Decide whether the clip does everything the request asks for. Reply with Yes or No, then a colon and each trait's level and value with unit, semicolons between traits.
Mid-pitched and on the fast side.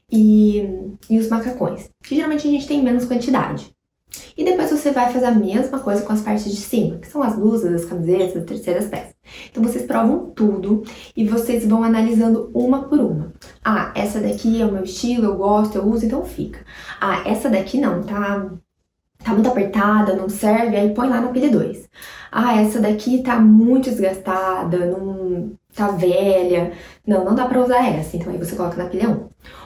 No: high, 215 Hz; fast, 195 wpm